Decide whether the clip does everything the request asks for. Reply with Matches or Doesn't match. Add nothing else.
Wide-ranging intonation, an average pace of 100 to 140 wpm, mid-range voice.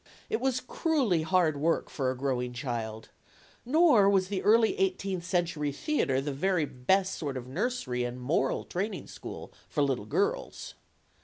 Doesn't match